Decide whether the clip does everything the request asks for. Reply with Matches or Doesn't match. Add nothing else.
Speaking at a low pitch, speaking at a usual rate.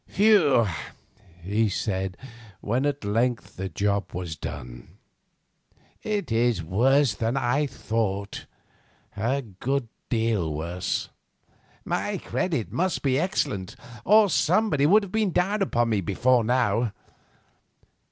Doesn't match